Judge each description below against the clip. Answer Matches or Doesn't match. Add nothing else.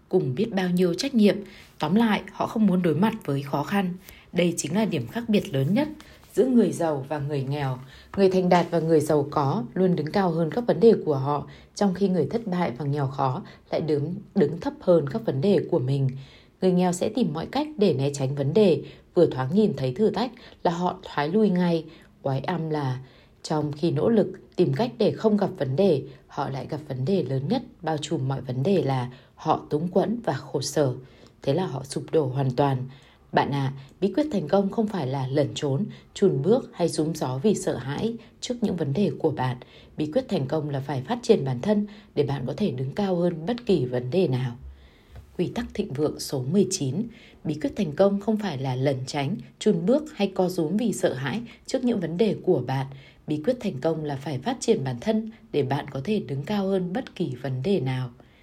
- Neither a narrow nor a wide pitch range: Doesn't match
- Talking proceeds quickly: Doesn't match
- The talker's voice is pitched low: Doesn't match